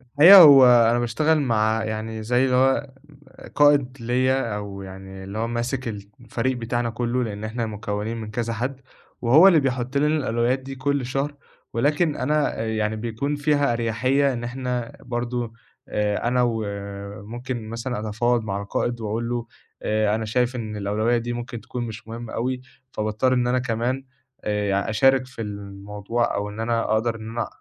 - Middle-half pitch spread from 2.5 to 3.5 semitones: Yes, average, 2.8 semitones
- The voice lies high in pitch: No, low, 120 Hz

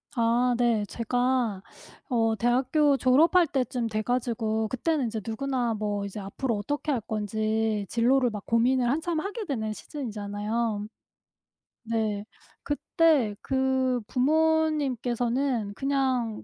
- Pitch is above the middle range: Yes, high, 240 Hz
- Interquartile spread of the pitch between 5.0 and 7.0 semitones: No, average, 3.6 semitones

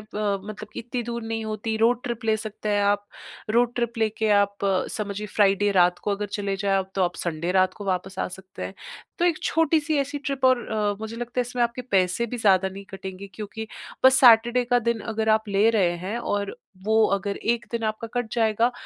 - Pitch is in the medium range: No, high, 215 Hz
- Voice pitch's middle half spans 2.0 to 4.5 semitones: Yes, average, 3.0 semitones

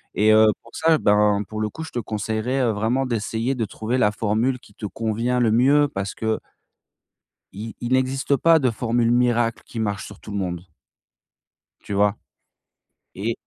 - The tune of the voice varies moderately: Yes, average, 3.0 semitones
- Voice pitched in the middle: No, low, 115 Hz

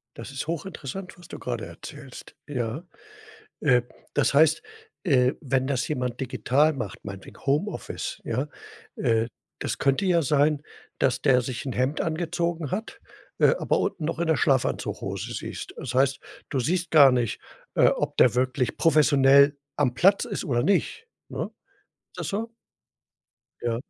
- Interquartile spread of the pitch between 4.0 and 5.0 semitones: Yes, average, 4.4 semitones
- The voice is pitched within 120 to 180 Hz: Yes, medium, 140 Hz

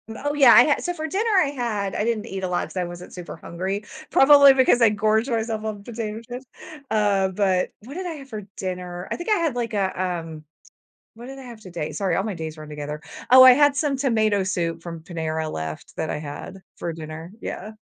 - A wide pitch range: Yes, wide, 6.1 semitones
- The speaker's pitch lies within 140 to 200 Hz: No, high, 210 Hz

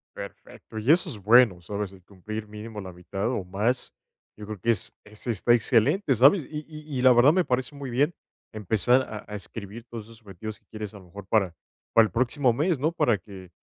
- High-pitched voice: No, low, 110 Hz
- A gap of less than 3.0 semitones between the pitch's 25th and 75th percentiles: No, average, 4.0 semitones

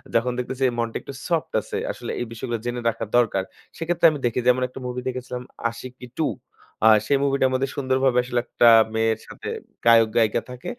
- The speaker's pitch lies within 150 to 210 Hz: No, low, 125 Hz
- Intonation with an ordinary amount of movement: No, narrow, 2.1 semitones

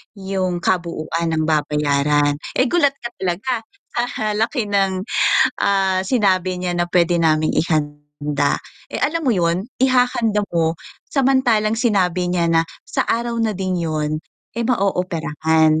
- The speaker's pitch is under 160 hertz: No, medium, 185 Hz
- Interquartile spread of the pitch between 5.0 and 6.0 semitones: Yes, wide, 5.4 semitones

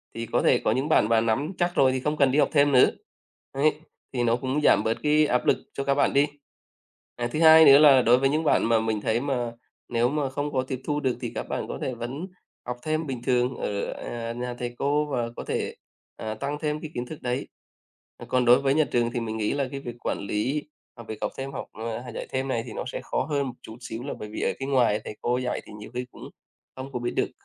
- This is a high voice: No, low, 130 Hz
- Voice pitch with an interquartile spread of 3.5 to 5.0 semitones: No, average, 3.1 semitones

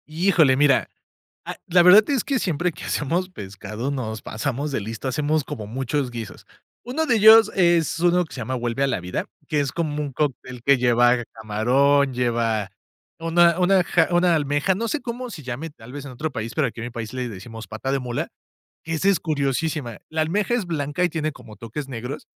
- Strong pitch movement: Yes, wide, 5.9 semitones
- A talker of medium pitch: Yes, medium, 145 Hz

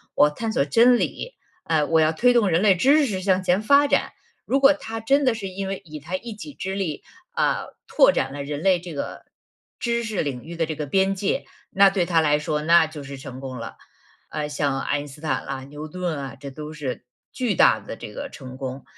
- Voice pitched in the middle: Yes, medium, 165 Hz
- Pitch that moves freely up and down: Yes, wide, 6.0 semitones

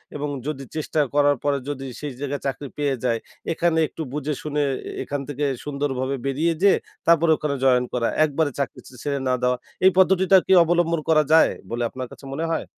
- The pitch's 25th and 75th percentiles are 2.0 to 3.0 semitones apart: Yes, average, 2.7 semitones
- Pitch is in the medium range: Yes, medium, 145 Hz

